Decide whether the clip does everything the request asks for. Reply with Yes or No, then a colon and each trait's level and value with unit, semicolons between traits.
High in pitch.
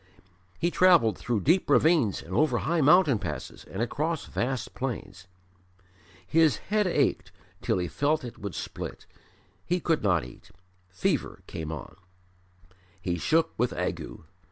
No: low, 125 Hz